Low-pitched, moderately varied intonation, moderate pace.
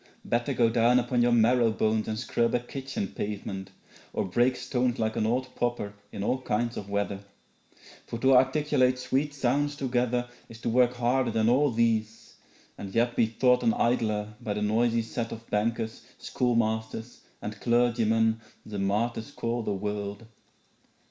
No: low, 115 Hz; narrow, 2.2 semitones; average, 160 wpm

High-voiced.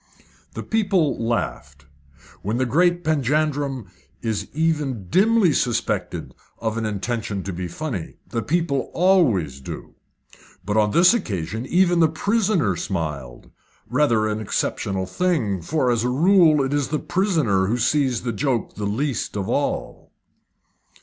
No: low, 125 Hz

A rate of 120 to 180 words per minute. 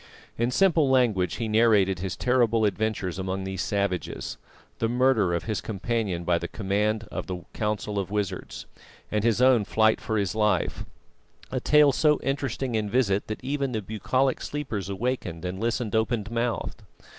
Yes: average, 160 wpm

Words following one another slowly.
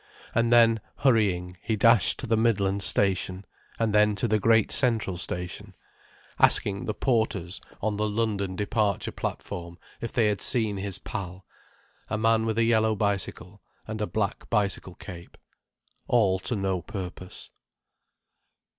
No: average, 145 wpm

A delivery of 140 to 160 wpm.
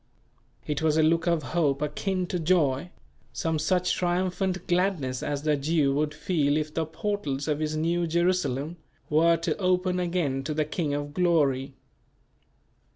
Yes: average, 155 wpm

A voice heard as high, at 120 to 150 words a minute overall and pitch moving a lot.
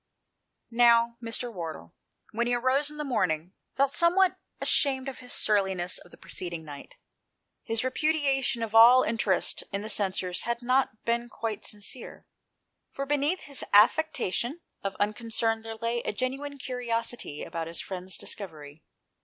No: high, 230 Hz; average, 145 wpm; average, 4.8 semitones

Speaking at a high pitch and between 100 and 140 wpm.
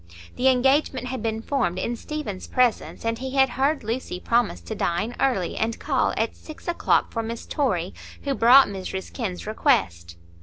No: high, 235 Hz; average, 175 wpm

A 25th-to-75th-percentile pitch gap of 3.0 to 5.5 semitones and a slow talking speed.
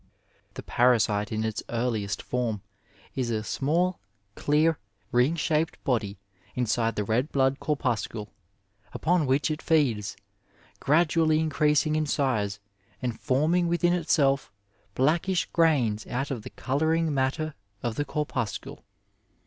Yes: average, 5.2 semitones; slow, 125 wpm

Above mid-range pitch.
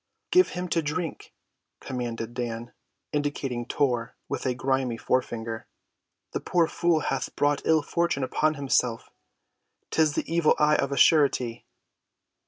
No: medium, 140 Hz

